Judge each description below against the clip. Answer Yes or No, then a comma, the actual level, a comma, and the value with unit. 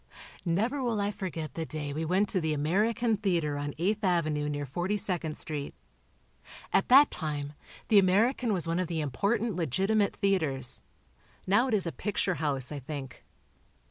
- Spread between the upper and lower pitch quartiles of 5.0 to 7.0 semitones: Yes, wide, 5.5 semitones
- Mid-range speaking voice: Yes, medium, 175 Hz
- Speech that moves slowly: No, average, 165 wpm